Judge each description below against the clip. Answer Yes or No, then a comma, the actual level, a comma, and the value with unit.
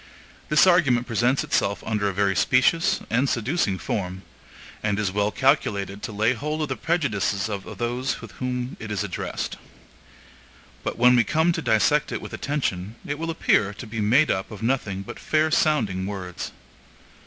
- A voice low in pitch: Yes, low, 115 Hz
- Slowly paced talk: No, average, 175 wpm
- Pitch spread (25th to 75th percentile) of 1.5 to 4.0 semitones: No, wide, 5.6 semitones